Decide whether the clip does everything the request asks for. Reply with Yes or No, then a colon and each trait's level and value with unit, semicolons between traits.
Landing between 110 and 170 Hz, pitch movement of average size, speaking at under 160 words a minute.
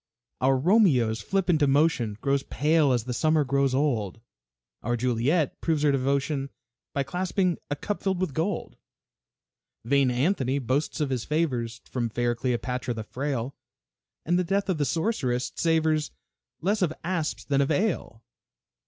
Yes: medium, 140 Hz; average, 4.5 semitones; average, 150 wpm